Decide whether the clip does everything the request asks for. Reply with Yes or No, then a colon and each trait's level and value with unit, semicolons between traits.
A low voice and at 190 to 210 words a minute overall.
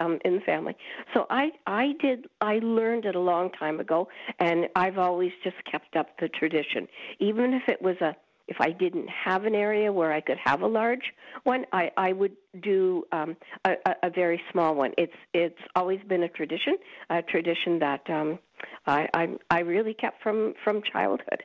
No: medium, 185 Hz; average, 195 wpm